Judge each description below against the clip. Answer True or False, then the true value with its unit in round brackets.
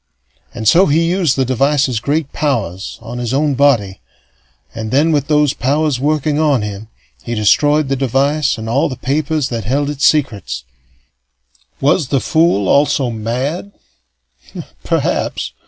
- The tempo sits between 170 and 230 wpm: False (145 wpm)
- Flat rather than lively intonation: False (4.0 semitones)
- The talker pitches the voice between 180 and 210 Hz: False (140 Hz)